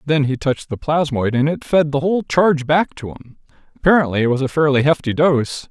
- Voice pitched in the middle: Yes, medium, 145 Hz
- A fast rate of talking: Yes, fast, 220 wpm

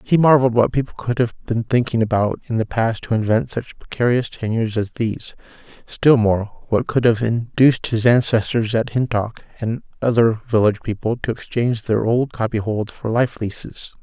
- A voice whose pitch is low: Yes, low, 115 Hz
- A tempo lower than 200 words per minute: Yes, average, 175 wpm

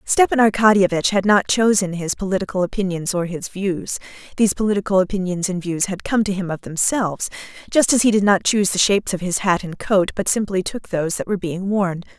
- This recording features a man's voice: No, female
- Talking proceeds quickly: Yes, fast, 210 wpm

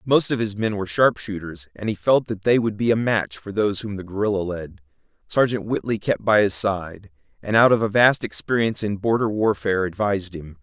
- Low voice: Yes, low, 100 Hz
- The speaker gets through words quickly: Yes, fast, 215 wpm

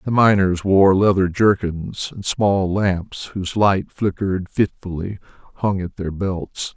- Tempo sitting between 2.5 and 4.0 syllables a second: Yes, 3.9 syllables/s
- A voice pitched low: Yes, very low, 95 Hz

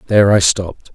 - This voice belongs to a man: Yes, male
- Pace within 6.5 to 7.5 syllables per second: Yes, 6.7 syllables/s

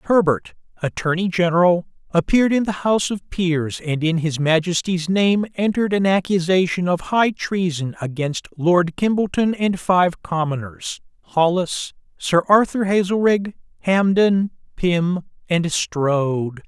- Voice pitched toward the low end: No, medium, 180 Hz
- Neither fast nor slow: No, slow, 120 wpm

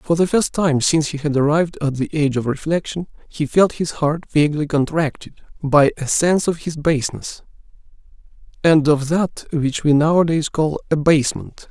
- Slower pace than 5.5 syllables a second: Yes, 5.2 syllables/s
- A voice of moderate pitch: Yes, medium, 155 Hz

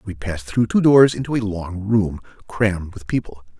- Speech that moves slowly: No, average, 200 wpm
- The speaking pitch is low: Yes, low, 100 Hz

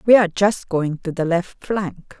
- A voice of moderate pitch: Yes, medium, 180 Hz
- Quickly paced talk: Yes, fast, 220 wpm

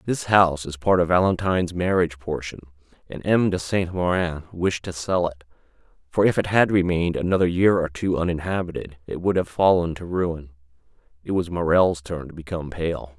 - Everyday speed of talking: Yes, average, 180 wpm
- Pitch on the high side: No, very low, 85 Hz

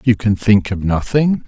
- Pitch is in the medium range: No, low, 110 Hz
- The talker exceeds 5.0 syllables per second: No, 4.4 syllables/s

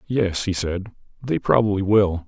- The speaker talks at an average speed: Yes, average, 160 wpm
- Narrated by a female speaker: No, male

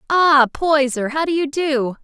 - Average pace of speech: Yes, average, 175 wpm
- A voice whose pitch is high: Yes, very high, 285 Hz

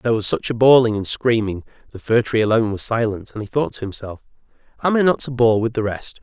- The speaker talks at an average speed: No, fast, 240 wpm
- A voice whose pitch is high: No, low, 115 Hz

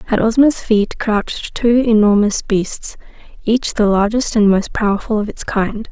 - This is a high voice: Yes, high, 215 Hz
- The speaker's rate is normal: Yes, average, 160 wpm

